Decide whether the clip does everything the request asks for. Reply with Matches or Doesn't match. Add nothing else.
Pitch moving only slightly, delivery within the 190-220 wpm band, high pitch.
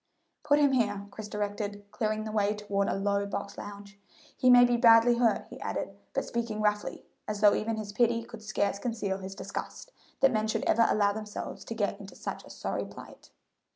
Matches